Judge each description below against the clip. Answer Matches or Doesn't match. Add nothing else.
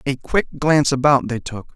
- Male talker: Matches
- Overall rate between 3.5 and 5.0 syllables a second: Doesn't match